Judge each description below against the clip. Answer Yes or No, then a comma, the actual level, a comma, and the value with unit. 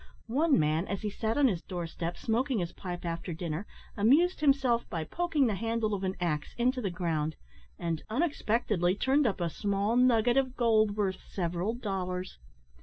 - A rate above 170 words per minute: Yes, average, 180 wpm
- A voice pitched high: Yes, high, 205 Hz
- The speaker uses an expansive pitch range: Yes, wide, 5.7 semitones